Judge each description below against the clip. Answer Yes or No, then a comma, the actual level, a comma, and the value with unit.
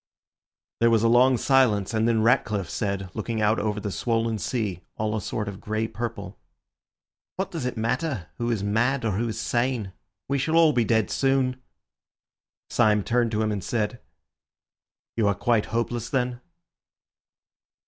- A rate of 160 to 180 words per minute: Yes, average, 165 wpm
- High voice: No, low, 115 Hz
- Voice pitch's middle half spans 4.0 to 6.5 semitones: No, average, 2.7 semitones